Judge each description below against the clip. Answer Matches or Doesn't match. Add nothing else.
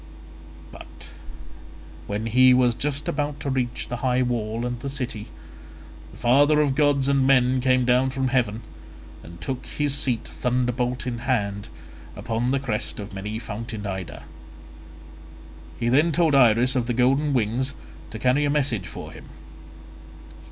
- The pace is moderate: Matches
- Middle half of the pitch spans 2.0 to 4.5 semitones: Matches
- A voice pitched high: Doesn't match